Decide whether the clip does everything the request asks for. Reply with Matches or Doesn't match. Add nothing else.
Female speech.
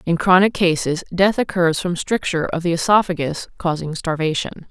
Matches